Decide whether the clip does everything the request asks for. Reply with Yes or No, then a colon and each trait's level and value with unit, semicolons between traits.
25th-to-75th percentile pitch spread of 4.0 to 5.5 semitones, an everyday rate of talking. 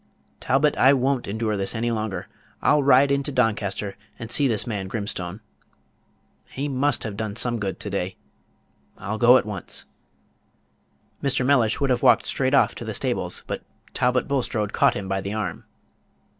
Yes: average, 4.5 semitones; average, 170 wpm